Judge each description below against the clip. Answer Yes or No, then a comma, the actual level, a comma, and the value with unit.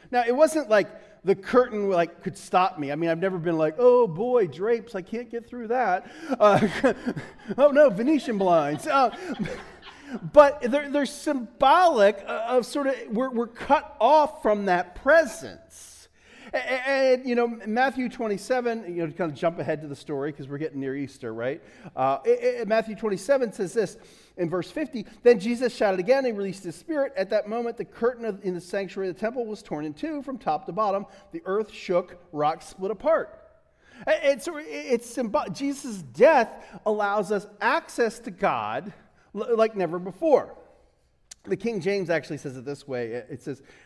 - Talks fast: No, average, 180 wpm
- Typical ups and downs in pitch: No, wide, 5.9 semitones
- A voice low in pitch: No, high, 220 Hz